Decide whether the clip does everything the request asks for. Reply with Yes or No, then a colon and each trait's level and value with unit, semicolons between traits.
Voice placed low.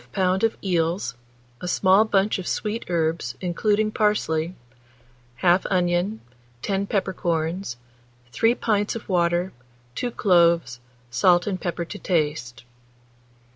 No: medium, 180 Hz